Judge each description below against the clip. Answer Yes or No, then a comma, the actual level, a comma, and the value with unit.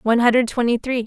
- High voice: Yes, high, 240 Hz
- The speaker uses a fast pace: Yes, fast, 225 wpm